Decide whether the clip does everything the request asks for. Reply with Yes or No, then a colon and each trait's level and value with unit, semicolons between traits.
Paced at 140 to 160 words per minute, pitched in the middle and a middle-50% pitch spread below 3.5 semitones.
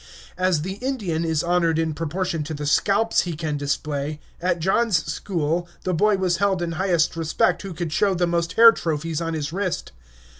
No: average, 190 wpm; medium, 170 Hz; average, 3.0 semitones